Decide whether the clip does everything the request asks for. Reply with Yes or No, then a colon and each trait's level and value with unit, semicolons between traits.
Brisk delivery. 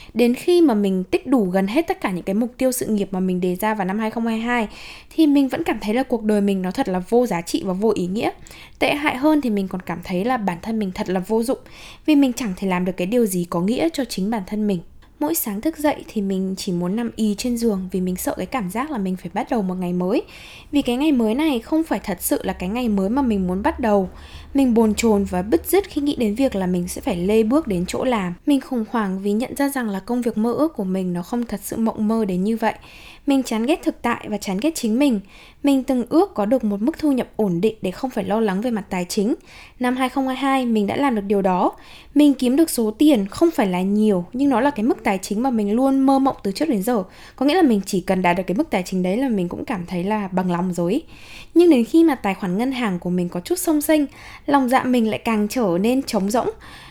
Yes: fast, 285 wpm